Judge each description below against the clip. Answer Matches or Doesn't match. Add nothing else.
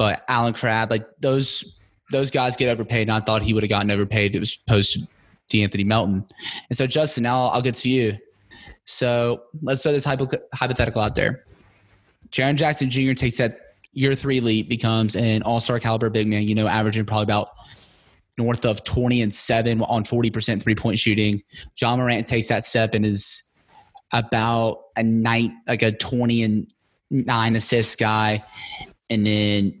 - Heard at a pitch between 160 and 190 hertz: Doesn't match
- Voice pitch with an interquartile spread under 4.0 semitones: Matches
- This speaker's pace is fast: Doesn't match